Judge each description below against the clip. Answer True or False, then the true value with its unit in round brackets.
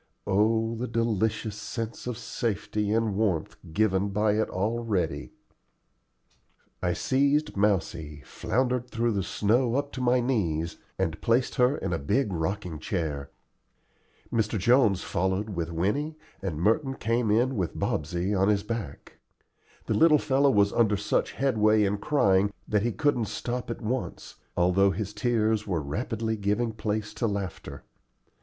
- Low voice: True (105 Hz)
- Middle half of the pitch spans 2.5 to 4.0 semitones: True (3.7 semitones)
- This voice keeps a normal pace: True (145 wpm)